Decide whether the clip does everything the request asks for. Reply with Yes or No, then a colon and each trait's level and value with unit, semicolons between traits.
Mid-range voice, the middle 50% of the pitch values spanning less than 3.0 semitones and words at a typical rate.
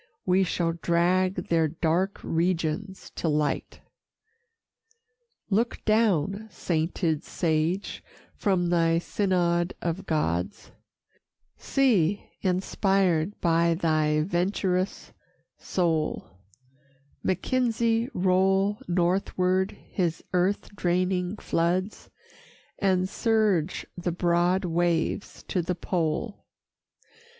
No: medium, 180 Hz; narrow, 2.5 semitones; slow, 85 wpm